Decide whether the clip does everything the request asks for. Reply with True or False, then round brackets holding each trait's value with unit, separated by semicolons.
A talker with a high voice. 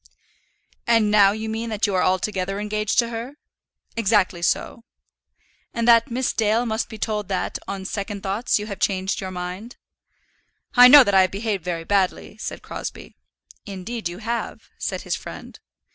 True (210 Hz)